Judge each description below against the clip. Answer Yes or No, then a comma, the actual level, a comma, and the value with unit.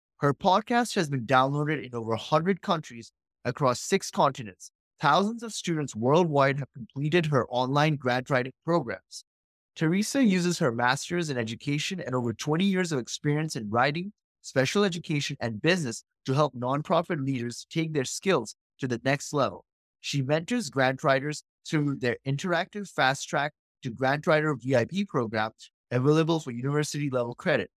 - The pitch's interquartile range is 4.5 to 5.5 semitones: Yes, average, 4.8 semitones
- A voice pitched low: No, medium, 145 Hz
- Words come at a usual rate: Yes, average, 155 wpm